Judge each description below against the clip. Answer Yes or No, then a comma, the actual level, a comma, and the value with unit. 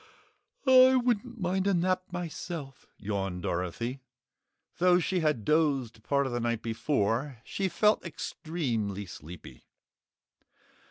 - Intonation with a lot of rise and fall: Yes, wide, 8.4 semitones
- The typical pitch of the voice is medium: Yes, medium, 145 Hz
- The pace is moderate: No, slow, 115 wpm